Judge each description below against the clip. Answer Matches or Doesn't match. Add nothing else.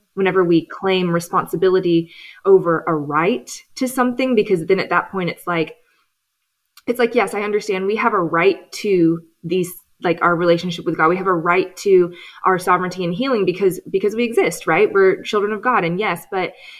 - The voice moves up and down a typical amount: Matches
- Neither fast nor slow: Matches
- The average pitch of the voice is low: Doesn't match